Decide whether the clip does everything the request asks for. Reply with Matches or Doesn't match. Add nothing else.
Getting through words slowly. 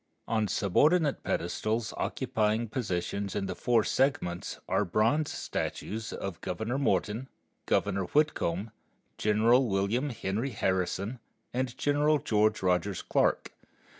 Matches